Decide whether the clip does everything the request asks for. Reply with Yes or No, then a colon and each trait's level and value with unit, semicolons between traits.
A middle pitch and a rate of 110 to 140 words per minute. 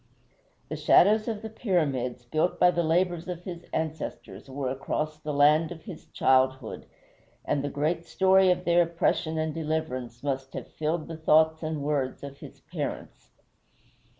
No: medium, 155 Hz; average, 160 wpm